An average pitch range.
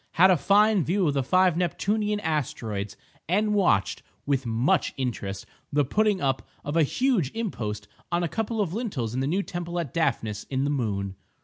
No: wide, 7.8 semitones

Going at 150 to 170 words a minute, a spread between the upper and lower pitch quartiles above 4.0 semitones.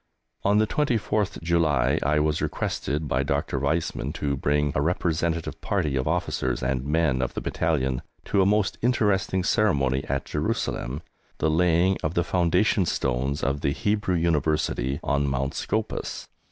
Yes: average, 155 wpm; average, 5.1 semitones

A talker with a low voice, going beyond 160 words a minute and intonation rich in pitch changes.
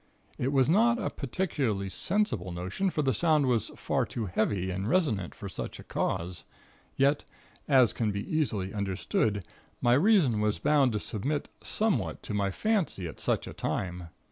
Yes: low, 120 Hz; average, 170 wpm; wide, 7.6 semitones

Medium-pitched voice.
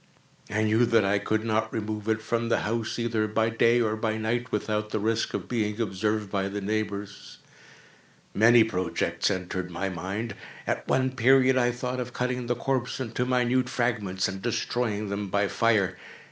No: low, 110 Hz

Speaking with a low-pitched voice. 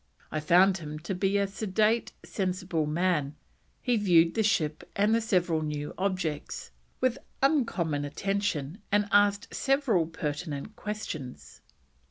No: medium, 185 Hz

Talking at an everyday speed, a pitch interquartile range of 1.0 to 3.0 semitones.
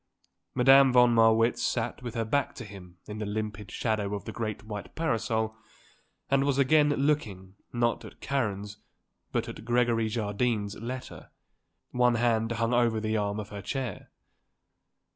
Yes: average, 155 wpm; average, 2.7 semitones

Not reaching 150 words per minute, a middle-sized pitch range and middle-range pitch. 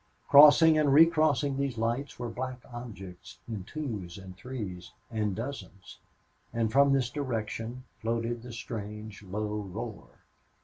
No: slow, 135 wpm; average, 4.5 semitones; low, 115 Hz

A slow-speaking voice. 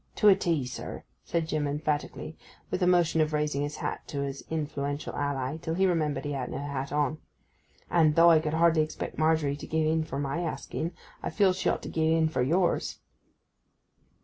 No: average, 200 wpm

